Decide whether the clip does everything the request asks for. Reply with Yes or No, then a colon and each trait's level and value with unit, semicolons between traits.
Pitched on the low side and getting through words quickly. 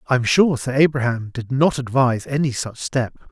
No: low, 130 Hz; average, 180 wpm